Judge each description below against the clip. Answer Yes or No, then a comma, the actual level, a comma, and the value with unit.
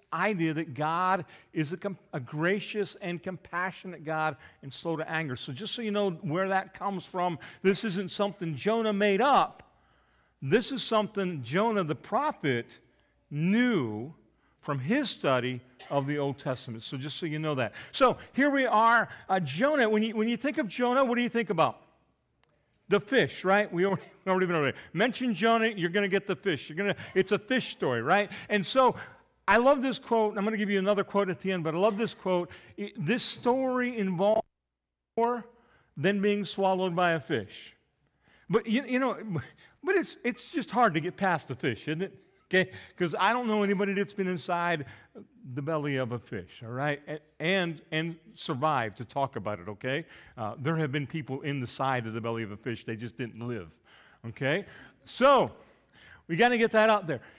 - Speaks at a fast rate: No, average, 195 wpm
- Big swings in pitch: Yes, wide, 6.2 semitones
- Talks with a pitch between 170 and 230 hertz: Yes, medium, 185 Hz